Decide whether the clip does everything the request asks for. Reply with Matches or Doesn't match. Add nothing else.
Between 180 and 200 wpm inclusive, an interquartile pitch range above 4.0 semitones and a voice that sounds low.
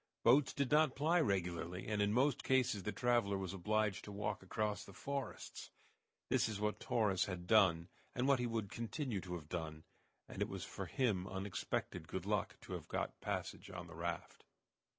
Matches